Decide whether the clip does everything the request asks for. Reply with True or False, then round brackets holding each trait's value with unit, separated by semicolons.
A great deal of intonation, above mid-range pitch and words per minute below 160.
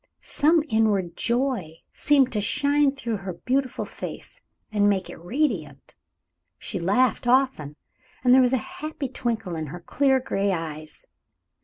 True (6.8 semitones; 230 Hz; 145 wpm)